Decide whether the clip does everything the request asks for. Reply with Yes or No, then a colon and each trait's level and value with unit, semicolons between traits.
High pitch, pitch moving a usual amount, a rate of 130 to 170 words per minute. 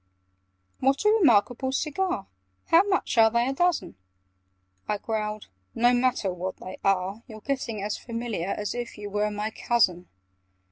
Yes: high, 225 Hz; average, 4.1 semitones; average, 155 wpm